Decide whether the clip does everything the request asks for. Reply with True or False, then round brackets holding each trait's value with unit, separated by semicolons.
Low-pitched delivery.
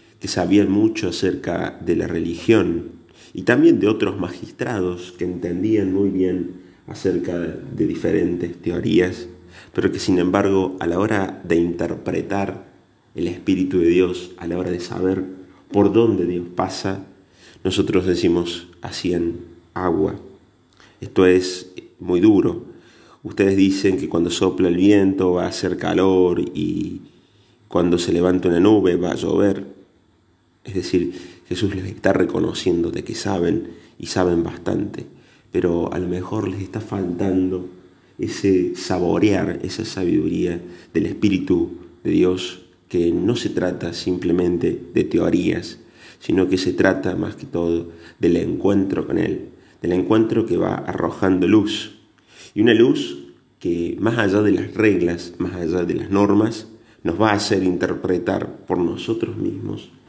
True (90 Hz)